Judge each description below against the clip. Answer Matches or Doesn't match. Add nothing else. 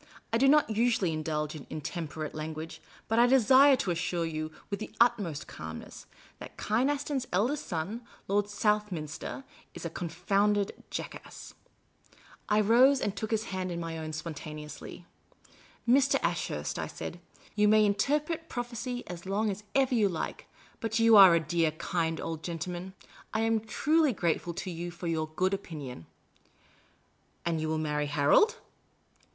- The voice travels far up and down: Matches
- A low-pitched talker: Doesn't match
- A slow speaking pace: Doesn't match